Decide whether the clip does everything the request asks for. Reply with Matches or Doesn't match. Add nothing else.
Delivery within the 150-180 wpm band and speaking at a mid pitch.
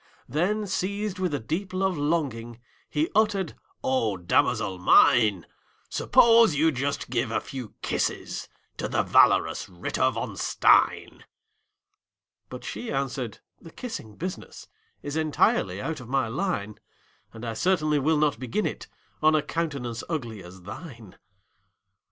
Doesn't match